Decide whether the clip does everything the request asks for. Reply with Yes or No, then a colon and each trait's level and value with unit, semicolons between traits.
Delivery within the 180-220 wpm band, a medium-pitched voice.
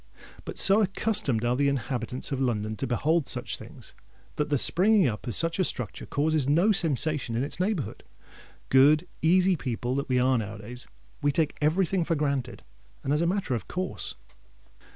Yes: average, 185 wpm; medium, 145 Hz